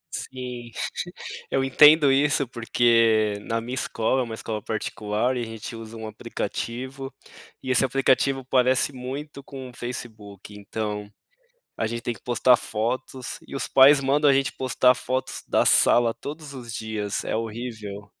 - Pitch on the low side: Yes, low, 120 Hz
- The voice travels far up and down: No, average, 3.0 semitones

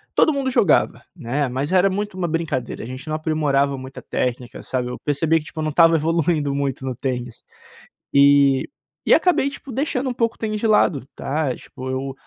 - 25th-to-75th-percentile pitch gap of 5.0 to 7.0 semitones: Yes, wide, 5.5 semitones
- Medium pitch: Yes, medium, 150 Hz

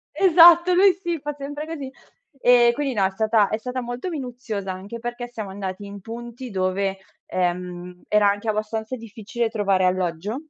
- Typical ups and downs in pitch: Yes, average, 4.8 semitones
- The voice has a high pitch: Yes, high, 225 Hz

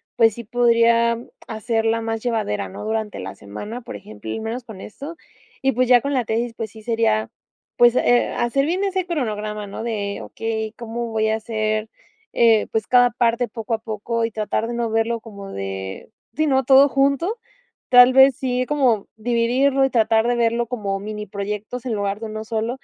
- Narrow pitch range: Yes, narrow, 2.3 semitones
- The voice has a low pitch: No, high, 230 Hz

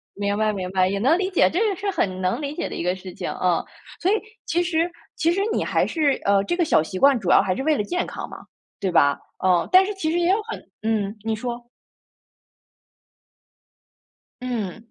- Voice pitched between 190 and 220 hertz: No, high, 240 Hz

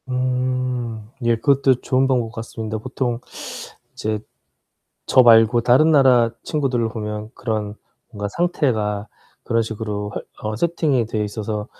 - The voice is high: No, low, 115 Hz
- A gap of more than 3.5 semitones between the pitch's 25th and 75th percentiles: No, average, 2.9 semitones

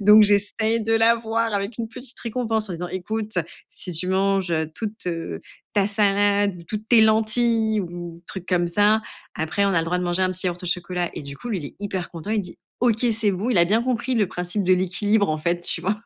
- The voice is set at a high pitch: Yes, high, 200 Hz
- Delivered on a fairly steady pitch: No, average, 3.8 semitones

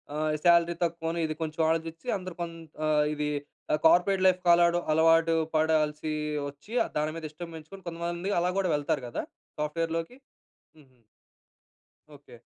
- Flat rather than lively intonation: Yes, narrow, 2.0 semitones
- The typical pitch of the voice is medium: Yes, medium, 165 Hz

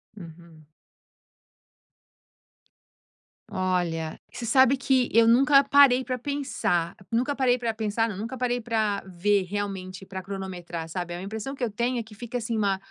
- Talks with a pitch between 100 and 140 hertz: No, high, 215 Hz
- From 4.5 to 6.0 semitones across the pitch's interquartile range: Yes, average, 4.9 semitones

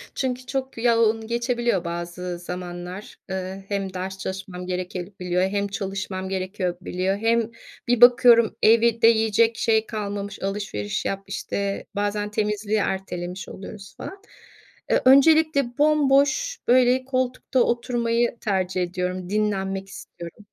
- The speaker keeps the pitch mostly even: No, average, 3.9 semitones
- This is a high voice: Yes, high, 205 Hz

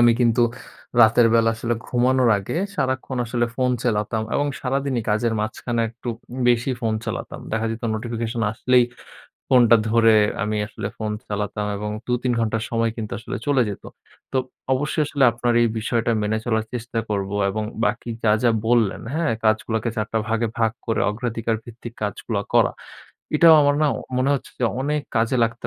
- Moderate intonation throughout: No, narrow, 2.1 semitones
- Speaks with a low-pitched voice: Yes, low, 115 Hz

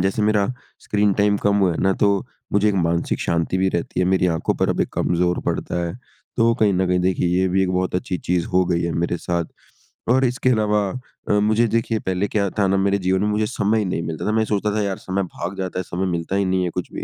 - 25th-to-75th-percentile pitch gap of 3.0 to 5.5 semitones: No, narrow, 2.5 semitones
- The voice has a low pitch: Yes, very low, 95 Hz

